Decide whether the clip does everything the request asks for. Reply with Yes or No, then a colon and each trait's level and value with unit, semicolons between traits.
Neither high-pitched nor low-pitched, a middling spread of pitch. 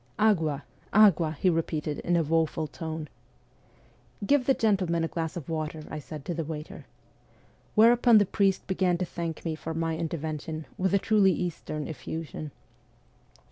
Yes: medium, 165 Hz; average, 3.3 semitones